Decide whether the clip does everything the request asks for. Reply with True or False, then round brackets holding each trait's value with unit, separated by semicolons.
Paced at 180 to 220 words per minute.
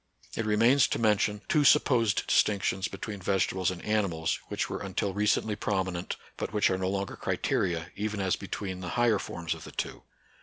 True (185 wpm)